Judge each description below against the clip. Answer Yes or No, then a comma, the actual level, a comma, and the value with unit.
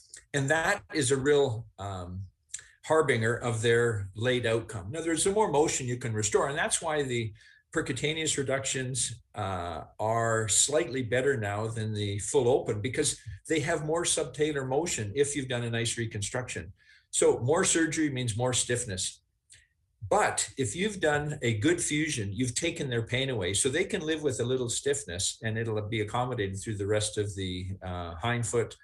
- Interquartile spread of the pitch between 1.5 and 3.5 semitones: No, wide, 5.6 semitones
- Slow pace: No, average, 175 wpm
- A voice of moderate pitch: No, low, 120 Hz